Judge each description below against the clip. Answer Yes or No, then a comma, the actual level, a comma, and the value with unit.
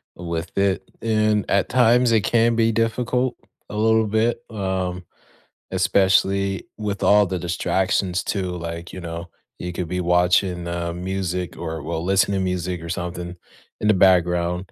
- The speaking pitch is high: No, very low, 95 Hz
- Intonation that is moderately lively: Yes, average, 3.1 semitones